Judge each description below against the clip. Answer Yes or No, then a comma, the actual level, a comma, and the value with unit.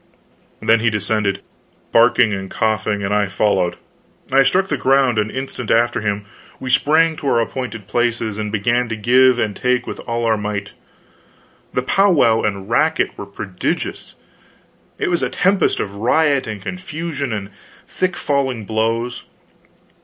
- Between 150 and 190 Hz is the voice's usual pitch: No, low, 115 Hz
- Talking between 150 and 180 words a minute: Yes, average, 155 wpm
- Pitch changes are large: No, average, 4.1 semitones